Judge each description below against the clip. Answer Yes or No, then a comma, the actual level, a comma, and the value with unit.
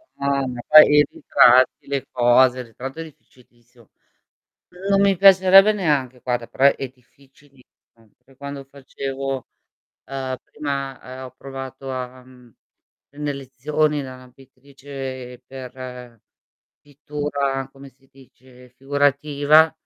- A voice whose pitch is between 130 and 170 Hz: Yes, low, 135 Hz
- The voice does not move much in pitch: Yes, narrow, 1.9 semitones